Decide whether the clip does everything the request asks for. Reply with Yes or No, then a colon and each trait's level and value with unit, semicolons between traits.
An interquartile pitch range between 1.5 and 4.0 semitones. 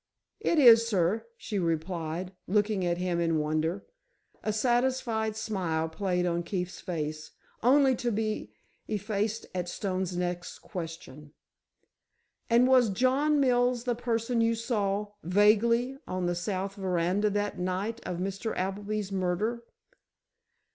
No: average, 4.4 semitones